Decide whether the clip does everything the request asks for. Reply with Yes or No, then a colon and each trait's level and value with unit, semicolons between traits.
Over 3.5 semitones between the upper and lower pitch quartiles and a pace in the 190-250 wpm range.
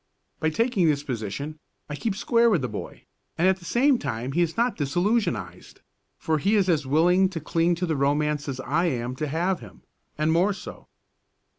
Yes: average, 5.1 semitones; average, 195 wpm